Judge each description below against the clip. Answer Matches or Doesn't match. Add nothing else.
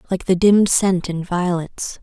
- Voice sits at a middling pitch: Matches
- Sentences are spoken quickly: Doesn't match